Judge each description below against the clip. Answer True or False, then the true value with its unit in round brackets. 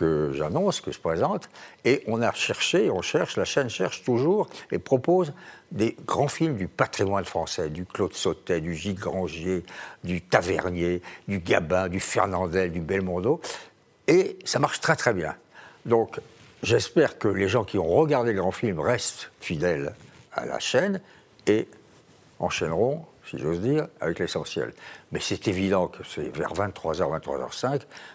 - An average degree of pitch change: False (9.0 semitones)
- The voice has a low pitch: True (95 Hz)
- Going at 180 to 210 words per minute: False (160 wpm)